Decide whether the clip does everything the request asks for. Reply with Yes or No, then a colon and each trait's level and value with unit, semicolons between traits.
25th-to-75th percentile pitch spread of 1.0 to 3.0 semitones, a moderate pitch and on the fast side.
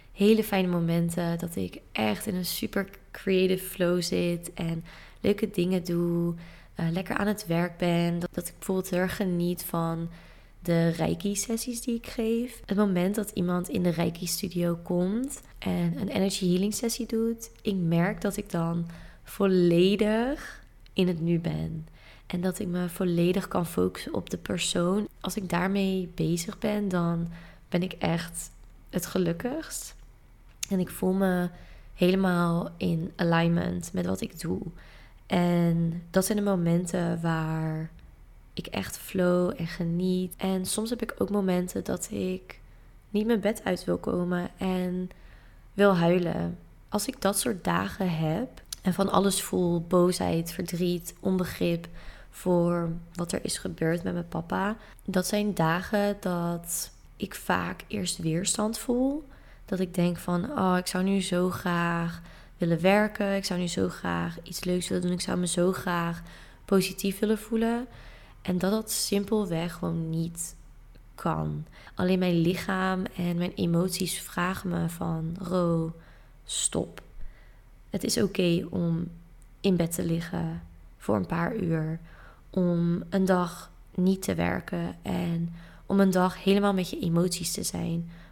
No: narrow, 2.4 semitones; medium, 180 Hz; average, 155 wpm